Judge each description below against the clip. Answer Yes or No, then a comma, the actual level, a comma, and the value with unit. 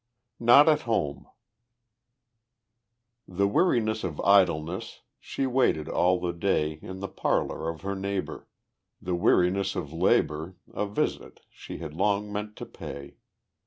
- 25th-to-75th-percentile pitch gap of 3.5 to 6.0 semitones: Yes, average, 3.8 semitones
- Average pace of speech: No, slow, 130 wpm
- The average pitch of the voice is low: Yes, very low, 95 Hz